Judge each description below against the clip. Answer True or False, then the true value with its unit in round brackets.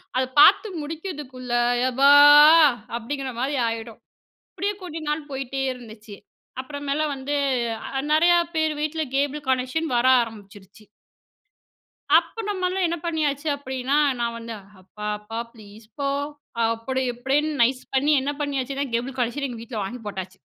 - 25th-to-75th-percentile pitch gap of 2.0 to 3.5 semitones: False (4.2 semitones)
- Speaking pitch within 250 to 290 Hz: True (265 Hz)